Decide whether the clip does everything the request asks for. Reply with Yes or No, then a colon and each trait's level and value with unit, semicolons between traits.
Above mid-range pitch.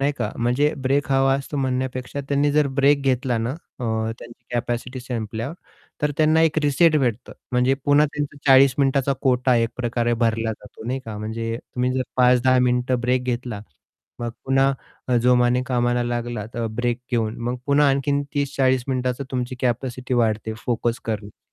No: low, 125 Hz